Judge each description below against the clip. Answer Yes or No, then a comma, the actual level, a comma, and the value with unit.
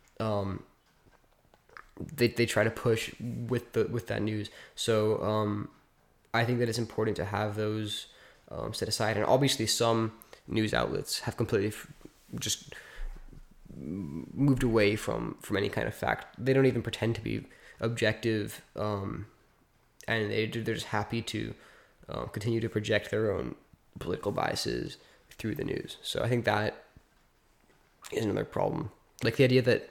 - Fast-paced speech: No, average, 155 wpm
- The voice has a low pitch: Yes, low, 110 Hz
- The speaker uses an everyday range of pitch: No, narrow, 1.7 semitones